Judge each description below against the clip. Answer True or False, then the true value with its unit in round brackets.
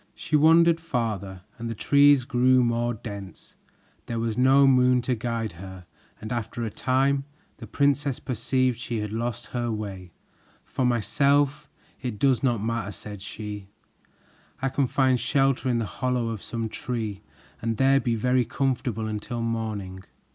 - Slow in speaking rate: False (155 wpm)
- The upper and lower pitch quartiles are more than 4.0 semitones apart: False (3.2 semitones)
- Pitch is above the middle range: False (120 Hz)